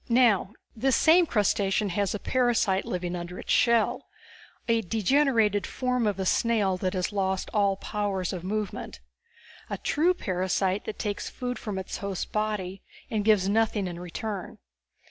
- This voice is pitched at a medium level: No, high, 205 Hz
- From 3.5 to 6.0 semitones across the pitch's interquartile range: No, average, 3.1 semitones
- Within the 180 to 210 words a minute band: No, average, 155 wpm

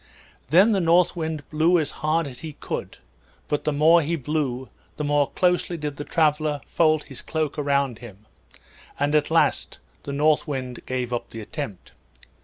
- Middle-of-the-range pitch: Yes, medium, 150 Hz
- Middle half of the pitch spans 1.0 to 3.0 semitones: Yes, narrow, 2.4 semitones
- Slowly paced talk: No, average, 175 wpm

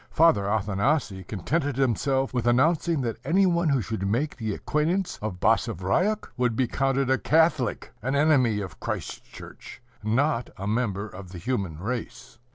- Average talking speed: Yes, average, 160 wpm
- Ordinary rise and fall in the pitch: No, wide, 6.2 semitones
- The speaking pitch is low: Yes, low, 125 Hz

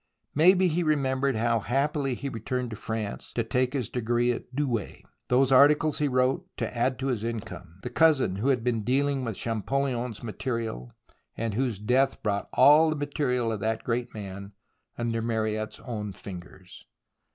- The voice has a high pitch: No, low, 120 Hz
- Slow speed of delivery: No, average, 165 wpm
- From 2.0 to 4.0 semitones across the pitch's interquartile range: Yes, average, 3.6 semitones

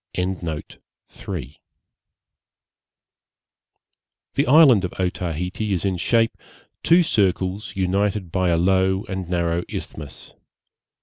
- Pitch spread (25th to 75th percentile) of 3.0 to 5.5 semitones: No, narrow, 2.6 semitones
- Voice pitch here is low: Yes, very low, 95 Hz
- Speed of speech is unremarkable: No, slow, 85 wpm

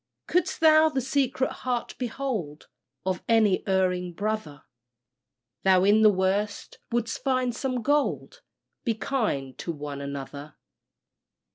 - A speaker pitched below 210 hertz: No, high, 215 Hz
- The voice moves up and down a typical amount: No, wide, 6.3 semitones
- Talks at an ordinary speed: No, slow, 120 wpm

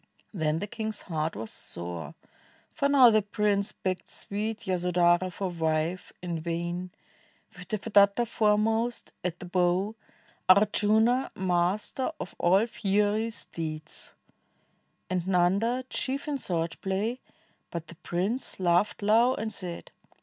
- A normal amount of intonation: Yes, average, 3.9 semitones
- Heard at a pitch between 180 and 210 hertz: Yes, high, 190 Hz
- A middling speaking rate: No, slow, 130 wpm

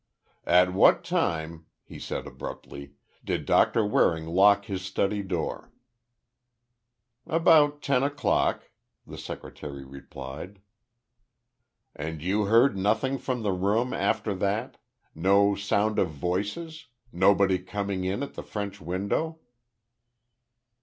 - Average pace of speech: No, slow, 110 wpm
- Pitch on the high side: No, low, 100 Hz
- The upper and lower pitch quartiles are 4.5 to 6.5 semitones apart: No, average, 3.7 semitones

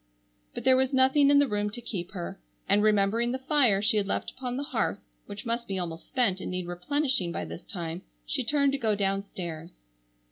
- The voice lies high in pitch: Yes, high, 210 Hz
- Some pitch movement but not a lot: No, wide, 5.9 semitones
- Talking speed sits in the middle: No, fast, 210 wpm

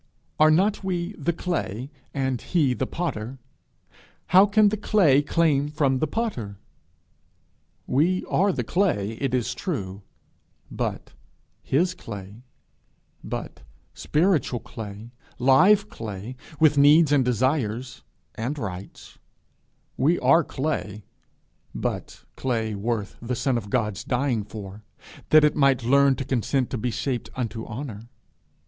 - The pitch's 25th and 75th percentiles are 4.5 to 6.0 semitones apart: Yes, wide, 5.6 semitones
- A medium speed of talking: No, slow, 130 wpm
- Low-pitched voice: Yes, low, 130 Hz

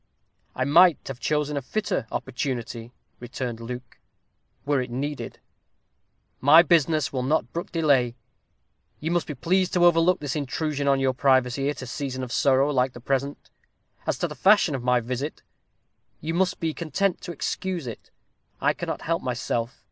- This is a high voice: No, medium, 140 Hz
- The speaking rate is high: No, average, 165 wpm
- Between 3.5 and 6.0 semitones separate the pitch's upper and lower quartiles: Yes, average, 4.4 semitones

